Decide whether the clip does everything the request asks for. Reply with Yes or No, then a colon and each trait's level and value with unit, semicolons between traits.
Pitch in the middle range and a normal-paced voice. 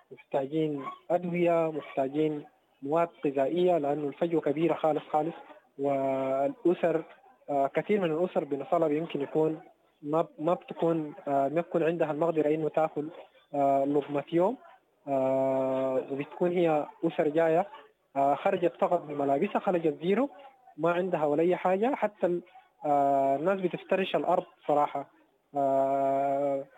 No: medium, 160 Hz; slow, 105 wpm